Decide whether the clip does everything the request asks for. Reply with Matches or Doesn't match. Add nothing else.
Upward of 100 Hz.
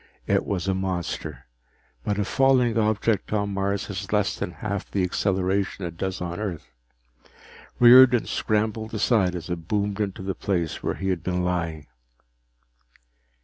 Doesn't match